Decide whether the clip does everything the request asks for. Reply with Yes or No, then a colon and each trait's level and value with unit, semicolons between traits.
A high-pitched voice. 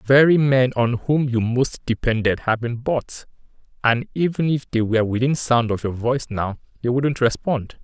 No: low, 125 Hz